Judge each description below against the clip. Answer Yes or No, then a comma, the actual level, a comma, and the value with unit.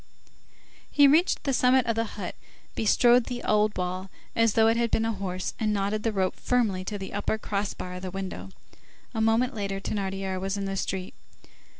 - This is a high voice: Yes, high, 210 Hz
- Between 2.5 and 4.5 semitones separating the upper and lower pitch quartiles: Yes, average, 2.9 semitones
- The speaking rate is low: No, average, 200 wpm